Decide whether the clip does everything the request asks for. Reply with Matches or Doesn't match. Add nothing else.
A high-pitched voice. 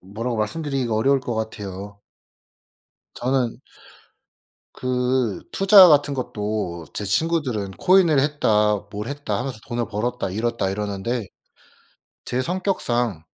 Doesn't match